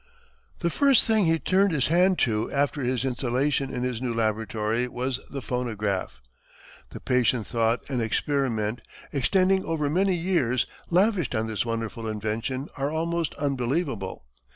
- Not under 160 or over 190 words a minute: No, average, 145 wpm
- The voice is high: No, low, 130 Hz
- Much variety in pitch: Yes, wide, 6.1 semitones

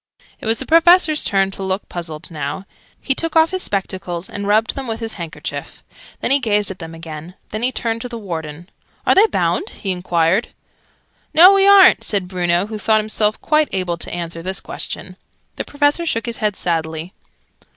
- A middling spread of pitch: No, wide, 6.6 semitones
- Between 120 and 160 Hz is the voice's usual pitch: No, high, 205 Hz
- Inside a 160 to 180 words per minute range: No, average, 195 wpm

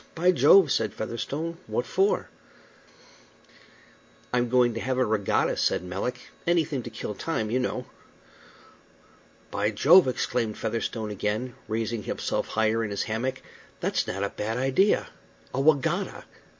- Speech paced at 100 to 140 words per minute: Yes, slow, 135 wpm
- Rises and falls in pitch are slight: No, average, 3.7 semitones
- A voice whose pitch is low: Yes, low, 120 Hz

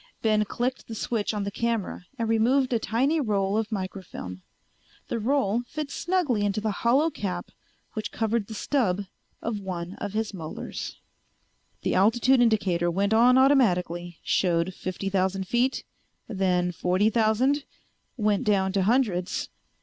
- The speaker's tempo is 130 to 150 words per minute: Yes, average, 145 wpm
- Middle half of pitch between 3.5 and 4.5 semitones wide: Yes, average, 4.0 semitones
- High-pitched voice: Yes, high, 215 Hz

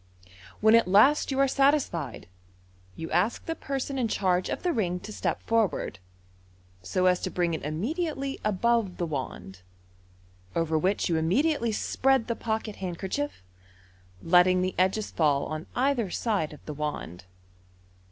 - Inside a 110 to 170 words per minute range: Yes, average, 150 wpm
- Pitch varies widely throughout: Yes, wide, 6.6 semitones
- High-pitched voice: Yes, high, 195 Hz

